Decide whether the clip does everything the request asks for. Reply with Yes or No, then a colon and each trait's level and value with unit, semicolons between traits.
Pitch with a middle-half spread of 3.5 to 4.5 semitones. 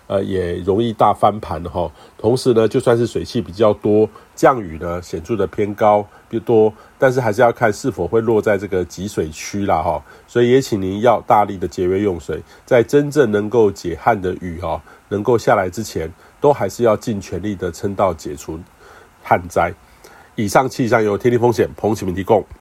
Yes: average, 4.1 semitones